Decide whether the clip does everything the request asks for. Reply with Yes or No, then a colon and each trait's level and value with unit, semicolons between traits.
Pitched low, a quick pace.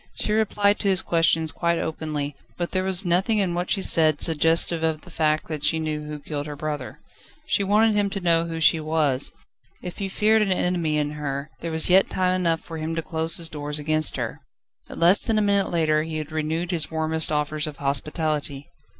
No: medium, 160 Hz; fast, 215 wpm